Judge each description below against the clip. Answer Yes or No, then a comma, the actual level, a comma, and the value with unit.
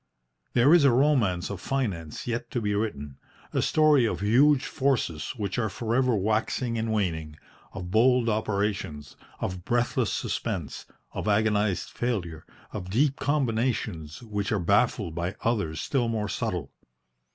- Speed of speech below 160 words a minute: Yes, average, 145 wpm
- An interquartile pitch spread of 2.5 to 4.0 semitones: No, average, 4.8 semitones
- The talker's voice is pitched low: Yes, low, 110 Hz